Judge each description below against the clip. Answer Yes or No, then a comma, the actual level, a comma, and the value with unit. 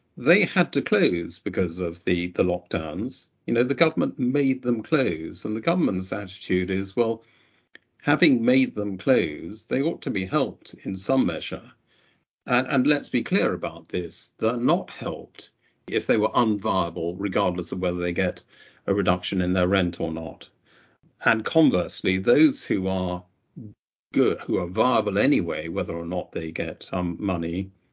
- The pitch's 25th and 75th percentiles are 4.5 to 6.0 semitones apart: No, average, 4.0 semitones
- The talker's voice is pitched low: Yes, very low, 95 Hz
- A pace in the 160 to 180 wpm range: Yes, average, 170 wpm